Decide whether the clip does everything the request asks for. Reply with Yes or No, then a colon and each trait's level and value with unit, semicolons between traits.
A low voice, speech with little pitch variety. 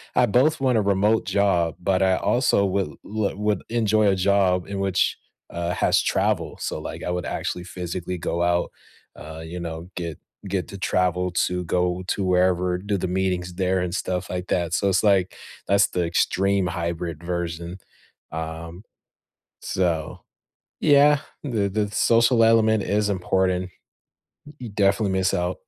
Yes: very low, 95 Hz; narrow, 2.3 semitones